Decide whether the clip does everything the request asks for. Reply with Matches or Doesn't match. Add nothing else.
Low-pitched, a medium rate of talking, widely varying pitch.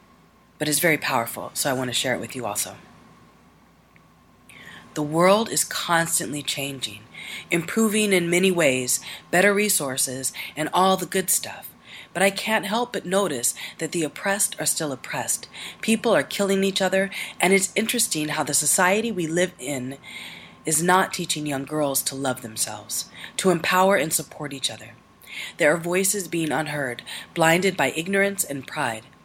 Doesn't match